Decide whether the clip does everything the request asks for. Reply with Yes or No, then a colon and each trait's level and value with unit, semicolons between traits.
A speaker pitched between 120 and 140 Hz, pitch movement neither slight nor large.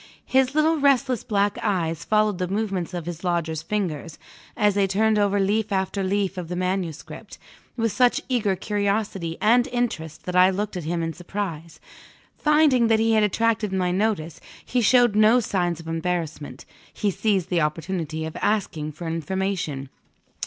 No: high, 195 Hz; average, 4.3 semitones